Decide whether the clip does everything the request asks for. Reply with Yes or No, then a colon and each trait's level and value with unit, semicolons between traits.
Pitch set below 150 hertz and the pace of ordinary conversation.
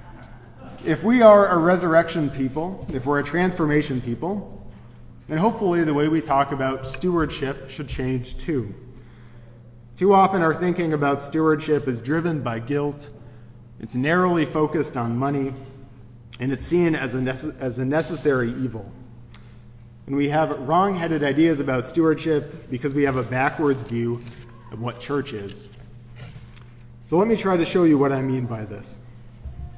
Yes: low, 135 Hz; average, 155 wpm